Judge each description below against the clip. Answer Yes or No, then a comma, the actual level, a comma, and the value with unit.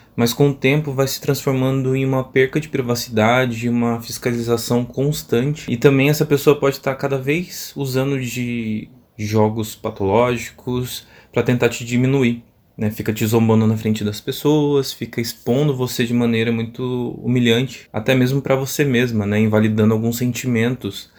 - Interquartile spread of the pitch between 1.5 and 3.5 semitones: Yes, average, 2.9 semitones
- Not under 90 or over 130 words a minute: No, average, 155 wpm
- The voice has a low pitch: Yes, low, 120 Hz